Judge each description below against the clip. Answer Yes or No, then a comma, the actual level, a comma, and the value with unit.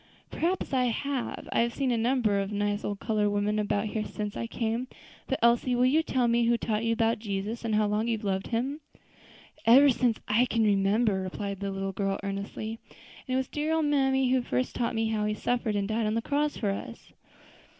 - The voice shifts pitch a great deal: No, average, 3.3 semitones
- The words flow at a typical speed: No, fast, 225 wpm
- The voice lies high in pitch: Yes, high, 225 Hz